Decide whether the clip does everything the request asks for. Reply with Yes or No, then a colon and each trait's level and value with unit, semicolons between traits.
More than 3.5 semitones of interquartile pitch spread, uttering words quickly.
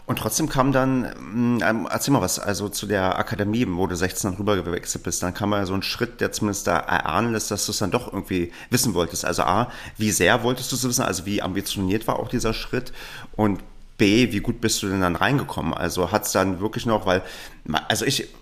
Yes: average, 4.1 semitones; fast, 230 wpm